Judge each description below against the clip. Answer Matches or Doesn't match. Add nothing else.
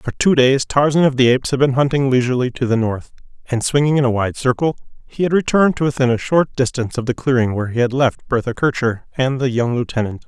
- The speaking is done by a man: Matches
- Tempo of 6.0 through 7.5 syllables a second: Matches